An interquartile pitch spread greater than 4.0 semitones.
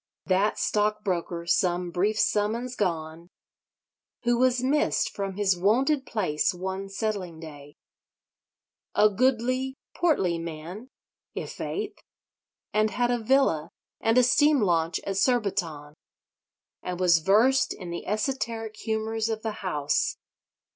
Yes: average, 5.3 semitones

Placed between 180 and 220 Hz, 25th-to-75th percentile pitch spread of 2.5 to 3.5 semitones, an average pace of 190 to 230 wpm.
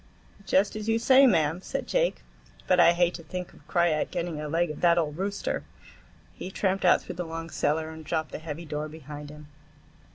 No: medium, 170 Hz; average, 2.9 semitones; fast, 205 wpm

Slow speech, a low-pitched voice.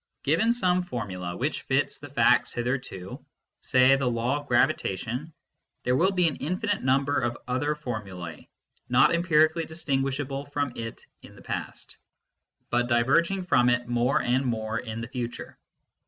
No: average, 155 wpm; low, 130 Hz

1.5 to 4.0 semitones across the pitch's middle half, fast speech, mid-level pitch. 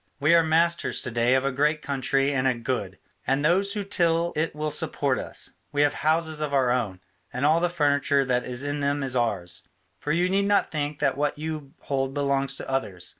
Yes: average, 3.1 semitones; fast, 220 wpm; medium, 145 Hz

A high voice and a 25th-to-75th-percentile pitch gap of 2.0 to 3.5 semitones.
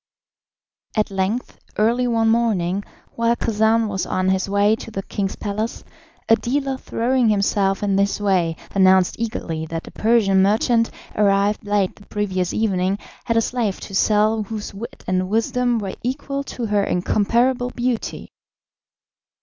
Yes: high, 210 Hz; average, 3.0 semitones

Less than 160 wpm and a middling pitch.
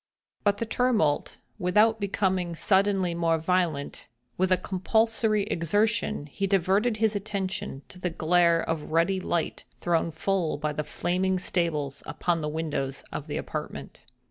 Yes: average, 145 wpm; medium, 180 Hz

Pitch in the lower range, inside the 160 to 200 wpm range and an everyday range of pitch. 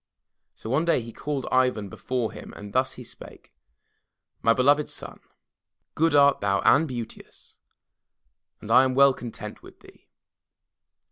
No: low, 130 Hz; average, 145 wpm; average, 3.6 semitones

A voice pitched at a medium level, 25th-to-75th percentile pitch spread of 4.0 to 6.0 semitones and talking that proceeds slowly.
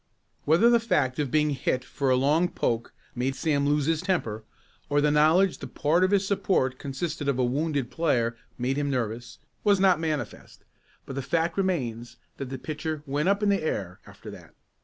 No: medium, 145 Hz; average, 4.6 semitones; average, 195 wpm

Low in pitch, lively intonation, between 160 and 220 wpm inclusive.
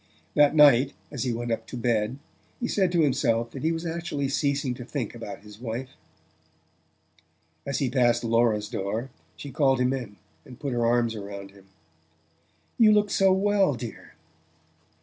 No: low, 125 Hz; average, 4.1 semitones; average, 170 wpm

